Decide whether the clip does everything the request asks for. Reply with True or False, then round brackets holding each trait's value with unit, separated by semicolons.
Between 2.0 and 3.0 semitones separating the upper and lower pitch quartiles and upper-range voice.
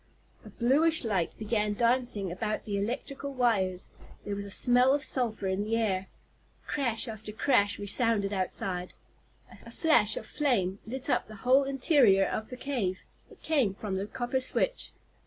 False (4.4 semitones; 220 Hz)